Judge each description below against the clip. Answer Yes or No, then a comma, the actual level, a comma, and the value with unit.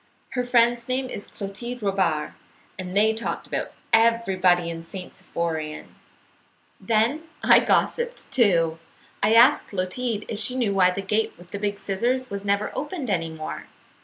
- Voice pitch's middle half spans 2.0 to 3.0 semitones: No, average, 4.6 semitones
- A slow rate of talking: No, average, 155 wpm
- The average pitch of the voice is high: Yes, high, 205 Hz